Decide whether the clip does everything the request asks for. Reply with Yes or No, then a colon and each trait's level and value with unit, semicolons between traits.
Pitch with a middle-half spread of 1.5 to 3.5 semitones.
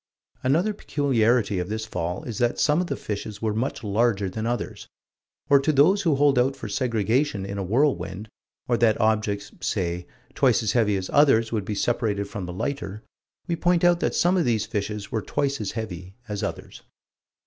No: wide, 5.4 semitones